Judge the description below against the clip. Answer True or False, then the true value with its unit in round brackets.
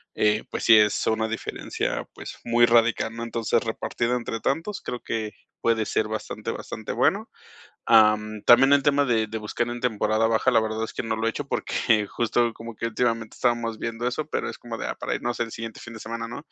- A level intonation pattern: True (1.4 semitones)